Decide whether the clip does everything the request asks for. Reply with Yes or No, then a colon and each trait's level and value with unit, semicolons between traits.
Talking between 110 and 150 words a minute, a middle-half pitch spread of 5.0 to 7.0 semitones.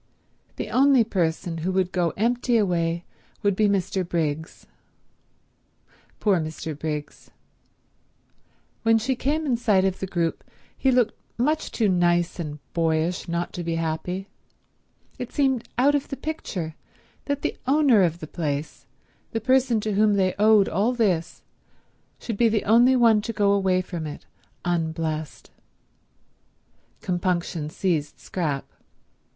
Yes: average, 140 wpm; wide, 5.5 semitones